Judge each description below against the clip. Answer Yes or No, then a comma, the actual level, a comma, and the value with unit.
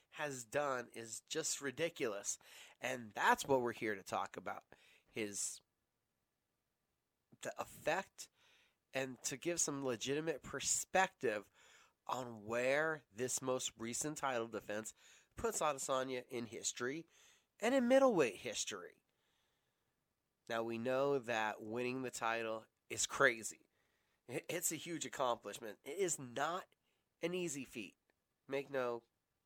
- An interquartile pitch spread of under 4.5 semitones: No, average, 4.8 semitones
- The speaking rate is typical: No, slow, 120 wpm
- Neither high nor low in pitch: No, low, 130 Hz